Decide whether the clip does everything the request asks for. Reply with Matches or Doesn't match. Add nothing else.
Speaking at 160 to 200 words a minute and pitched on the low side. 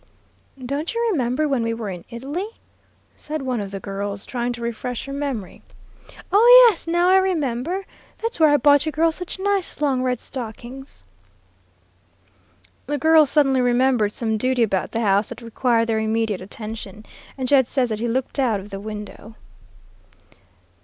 Doesn't match